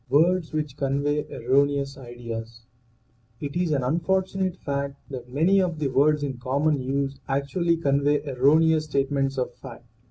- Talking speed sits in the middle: Yes, average, 150 wpm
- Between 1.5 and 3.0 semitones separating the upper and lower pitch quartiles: Yes, narrow, 2.6 semitones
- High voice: No, medium, 140 Hz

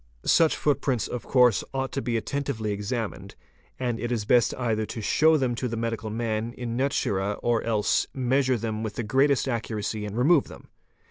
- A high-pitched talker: No, low, 120 Hz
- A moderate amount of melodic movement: Yes, average, 3.0 semitones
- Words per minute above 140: Yes, average, 185 wpm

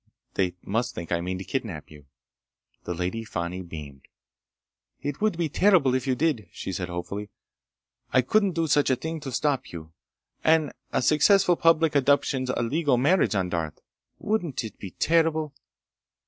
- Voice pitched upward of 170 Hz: No, low, 130 Hz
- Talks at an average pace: Yes, average, 160 wpm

